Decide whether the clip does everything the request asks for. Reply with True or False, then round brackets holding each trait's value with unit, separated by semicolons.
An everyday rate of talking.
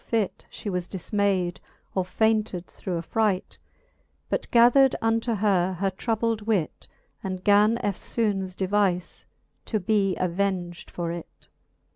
False (120 wpm)